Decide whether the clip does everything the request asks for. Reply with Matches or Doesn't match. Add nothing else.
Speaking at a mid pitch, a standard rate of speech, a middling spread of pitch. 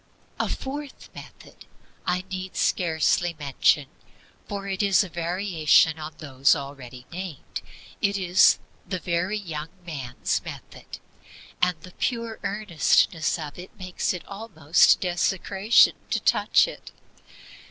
Doesn't match